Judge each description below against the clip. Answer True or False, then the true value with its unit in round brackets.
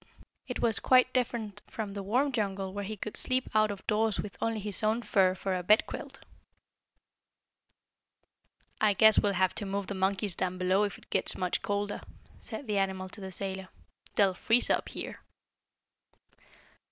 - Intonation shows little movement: True (2.3 semitones)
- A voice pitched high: True (205 Hz)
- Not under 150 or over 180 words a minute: True (175 wpm)